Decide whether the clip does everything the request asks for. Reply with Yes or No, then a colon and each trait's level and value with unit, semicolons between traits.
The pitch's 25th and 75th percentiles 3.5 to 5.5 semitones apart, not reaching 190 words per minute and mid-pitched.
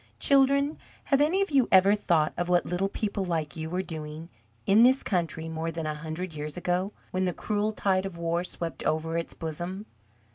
No: average, 3.9 semitones; average, 195 wpm; medium, 180 Hz